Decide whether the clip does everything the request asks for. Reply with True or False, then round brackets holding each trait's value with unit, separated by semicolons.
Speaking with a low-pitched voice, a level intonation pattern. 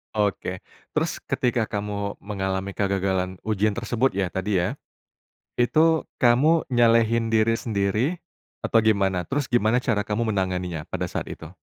False (105 Hz; 3.4 semitones)